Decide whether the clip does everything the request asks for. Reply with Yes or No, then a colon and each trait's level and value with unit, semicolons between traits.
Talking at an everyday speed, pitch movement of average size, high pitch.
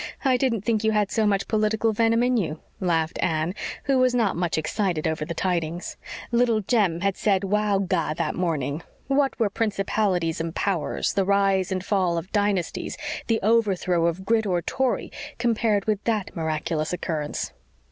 Yes: average, 170 wpm; average, 4.4 semitones; high, 195 Hz